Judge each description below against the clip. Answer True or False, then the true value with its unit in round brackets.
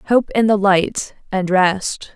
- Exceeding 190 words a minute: False (165 wpm)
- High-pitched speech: True (200 Hz)